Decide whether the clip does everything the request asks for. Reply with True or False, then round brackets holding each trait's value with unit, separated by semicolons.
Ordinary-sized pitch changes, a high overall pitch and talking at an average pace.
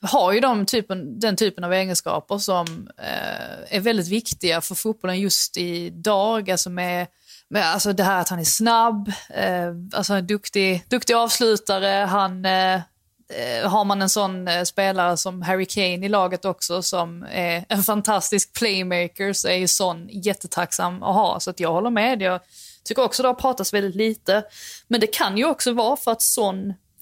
True (3.0 semitones; 195 Hz; 180 wpm)